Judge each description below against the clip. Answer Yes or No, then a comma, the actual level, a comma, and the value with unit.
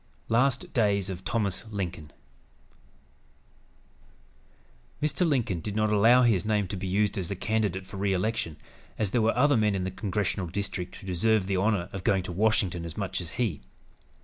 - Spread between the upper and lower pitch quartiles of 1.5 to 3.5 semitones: Yes, average, 3.0 semitones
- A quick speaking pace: No, average, 175 wpm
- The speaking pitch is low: Yes, low, 100 Hz